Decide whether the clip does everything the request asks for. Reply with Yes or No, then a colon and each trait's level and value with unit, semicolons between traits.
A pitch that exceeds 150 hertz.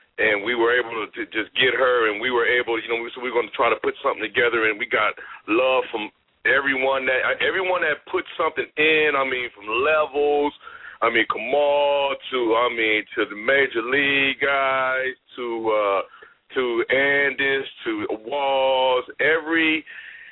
No: medium, 140 Hz